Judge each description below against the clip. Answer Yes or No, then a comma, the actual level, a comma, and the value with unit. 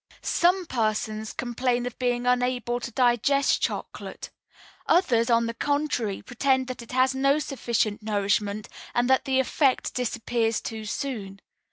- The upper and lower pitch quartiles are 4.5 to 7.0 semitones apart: No, average, 2.9 semitones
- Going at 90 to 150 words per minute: Yes, average, 140 wpm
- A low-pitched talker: No, high, 245 Hz